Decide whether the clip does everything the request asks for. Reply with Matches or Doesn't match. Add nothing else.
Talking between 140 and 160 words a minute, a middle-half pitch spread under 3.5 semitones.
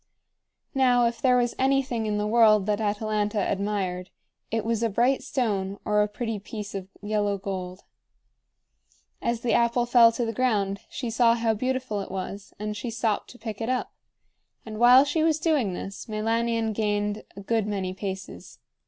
Doesn't match